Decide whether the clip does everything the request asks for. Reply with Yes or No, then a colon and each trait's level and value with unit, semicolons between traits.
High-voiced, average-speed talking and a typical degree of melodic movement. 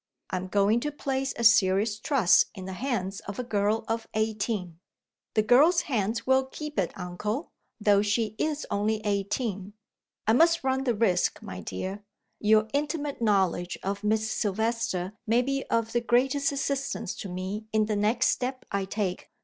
Yes: high, 220 Hz; average, 170 wpm; average, 4.2 semitones